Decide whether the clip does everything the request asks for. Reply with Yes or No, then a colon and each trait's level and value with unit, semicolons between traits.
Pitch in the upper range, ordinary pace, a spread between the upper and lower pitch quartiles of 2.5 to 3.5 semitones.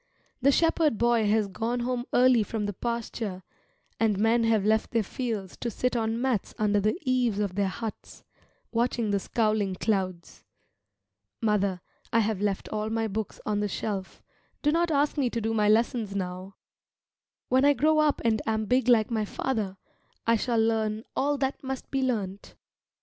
Yes: high, 225 Hz; average, 175 wpm; average, 3.0 semitones